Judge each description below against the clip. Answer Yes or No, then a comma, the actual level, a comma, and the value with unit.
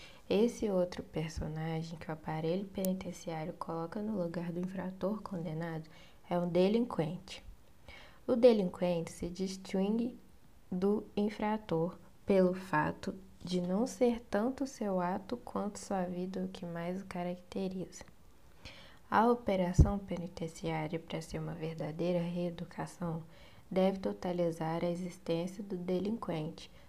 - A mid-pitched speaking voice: Yes, medium, 180 Hz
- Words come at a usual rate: No, slow, 115 wpm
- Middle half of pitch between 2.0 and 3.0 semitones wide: Yes, average, 2.7 semitones